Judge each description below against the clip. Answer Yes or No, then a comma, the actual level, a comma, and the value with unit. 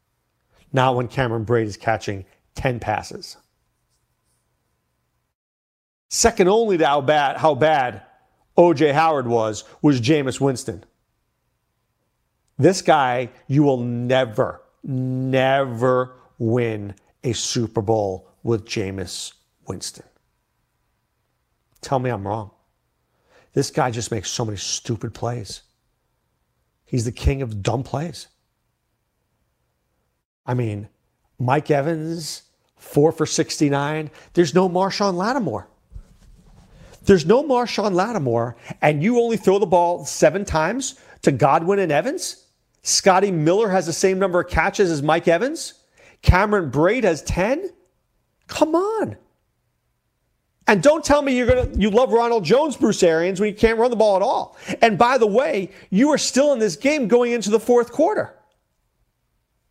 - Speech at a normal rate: No, slow, 130 wpm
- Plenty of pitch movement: Yes, wide, 9.0 semitones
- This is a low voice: No, medium, 155 Hz